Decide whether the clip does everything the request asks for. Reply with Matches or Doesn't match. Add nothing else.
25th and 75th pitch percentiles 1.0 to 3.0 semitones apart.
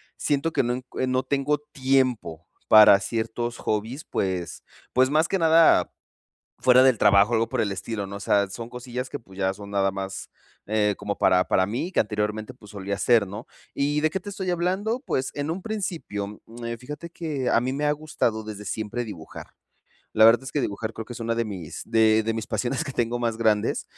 Doesn't match